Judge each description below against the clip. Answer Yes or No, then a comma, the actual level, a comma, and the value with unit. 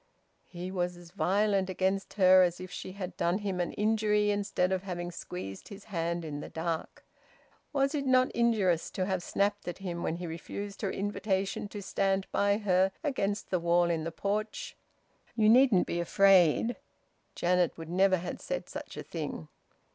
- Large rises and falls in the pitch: No, average, 2.8 semitones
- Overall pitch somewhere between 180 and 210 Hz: Yes, high, 190 Hz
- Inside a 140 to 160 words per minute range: No, average, 180 wpm